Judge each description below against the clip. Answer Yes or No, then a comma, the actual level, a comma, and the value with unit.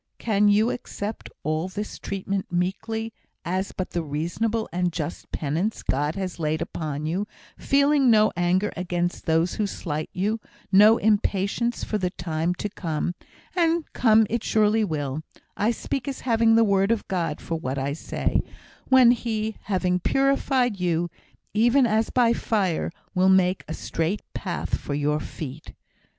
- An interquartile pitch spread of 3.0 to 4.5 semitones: No, average, 4.9 semitones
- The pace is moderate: Yes, average, 155 wpm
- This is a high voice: Yes, high, 195 Hz